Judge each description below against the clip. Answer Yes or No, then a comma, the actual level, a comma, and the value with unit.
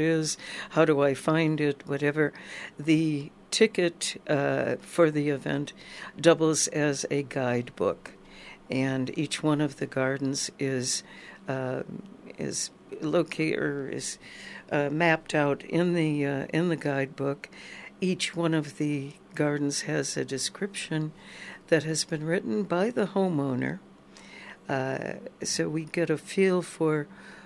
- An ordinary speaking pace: No, slow, 130 wpm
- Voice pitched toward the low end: No, medium, 155 Hz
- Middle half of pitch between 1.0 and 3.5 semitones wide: Yes, average, 3.1 semitones